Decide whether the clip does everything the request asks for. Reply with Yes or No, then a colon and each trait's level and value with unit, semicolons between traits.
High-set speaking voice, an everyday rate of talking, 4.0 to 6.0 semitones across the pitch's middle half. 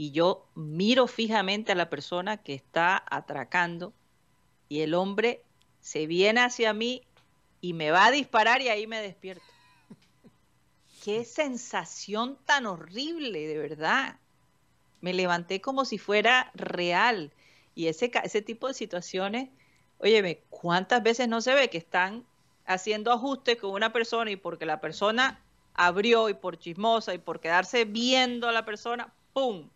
Yes: high, 210 Hz; average, 145 wpm; average, 5.2 semitones